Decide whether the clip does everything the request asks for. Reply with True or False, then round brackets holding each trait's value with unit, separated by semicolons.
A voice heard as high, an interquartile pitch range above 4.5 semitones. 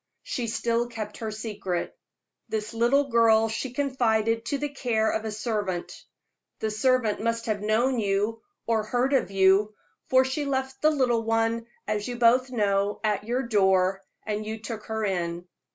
False (225 Hz; 2.5 semitones)